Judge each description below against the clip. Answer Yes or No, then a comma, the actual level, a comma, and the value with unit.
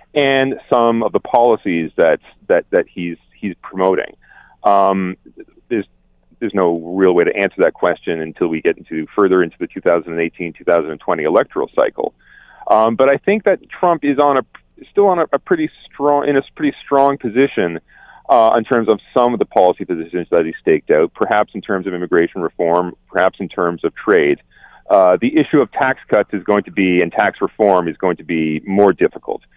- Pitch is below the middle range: Yes, low, 105 Hz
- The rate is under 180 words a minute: No, average, 195 wpm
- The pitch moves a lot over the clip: Yes, wide, 7.9 semitones